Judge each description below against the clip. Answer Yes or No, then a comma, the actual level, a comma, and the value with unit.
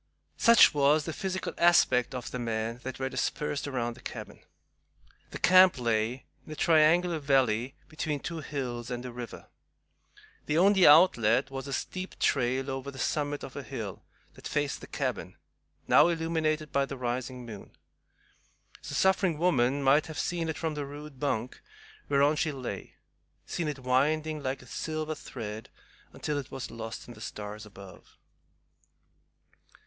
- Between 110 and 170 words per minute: Yes, average, 160 wpm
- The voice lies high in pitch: No, medium, 140 Hz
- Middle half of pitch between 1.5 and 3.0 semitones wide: No, average, 4.1 semitones